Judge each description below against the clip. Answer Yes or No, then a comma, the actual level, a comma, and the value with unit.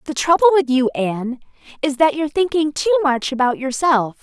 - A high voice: Yes, very high, 285 Hz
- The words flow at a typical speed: Yes, average, 185 wpm